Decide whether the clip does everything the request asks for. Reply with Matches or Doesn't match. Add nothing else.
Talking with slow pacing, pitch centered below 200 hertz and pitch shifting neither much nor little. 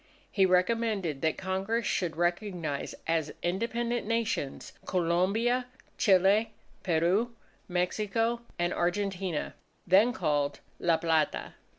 Matches